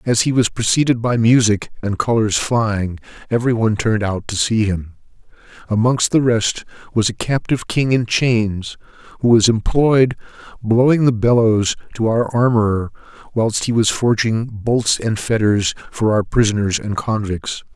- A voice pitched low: Yes, low, 115 Hz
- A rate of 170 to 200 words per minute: No, average, 155 wpm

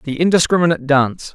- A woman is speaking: No, male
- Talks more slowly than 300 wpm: Yes, slow, 135 wpm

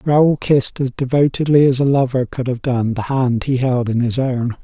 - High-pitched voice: No, low, 130 Hz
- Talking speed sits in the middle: No, fast, 220 wpm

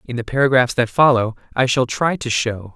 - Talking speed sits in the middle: No, fast, 220 wpm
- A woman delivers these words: No, male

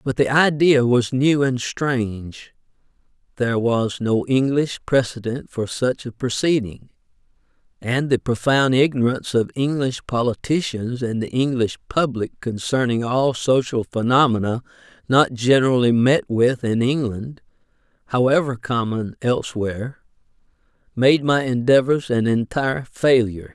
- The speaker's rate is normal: No, slow, 115 wpm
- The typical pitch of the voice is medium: No, low, 125 Hz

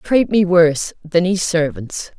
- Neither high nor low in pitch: Yes, medium, 170 Hz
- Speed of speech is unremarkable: Yes, average, 165 wpm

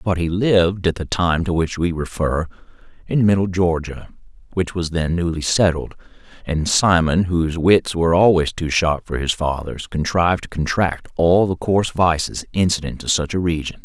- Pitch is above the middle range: No, very low, 85 Hz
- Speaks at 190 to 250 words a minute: No, average, 180 wpm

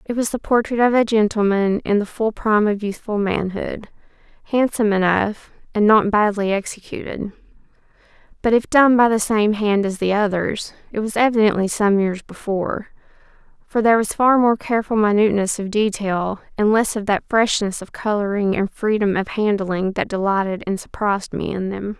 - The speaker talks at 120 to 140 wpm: No, average, 170 wpm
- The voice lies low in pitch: No, high, 210 Hz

